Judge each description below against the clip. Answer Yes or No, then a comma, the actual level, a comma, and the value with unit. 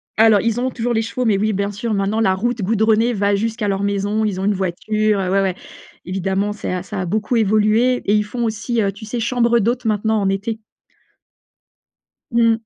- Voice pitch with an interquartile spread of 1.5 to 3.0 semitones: Yes, narrow, 2.4 semitones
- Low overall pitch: No, high, 215 Hz